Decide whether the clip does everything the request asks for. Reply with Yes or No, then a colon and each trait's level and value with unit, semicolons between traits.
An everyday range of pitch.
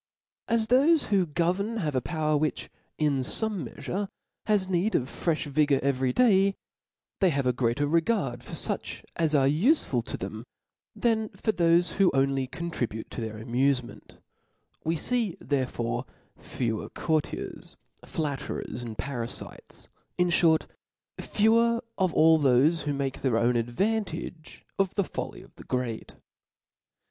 No: wide, 6.8 semitones